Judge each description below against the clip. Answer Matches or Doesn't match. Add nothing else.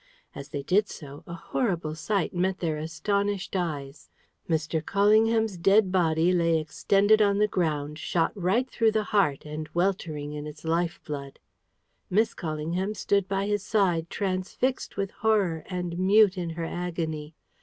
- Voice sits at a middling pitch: Matches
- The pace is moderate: Matches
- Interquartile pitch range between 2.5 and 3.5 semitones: Doesn't match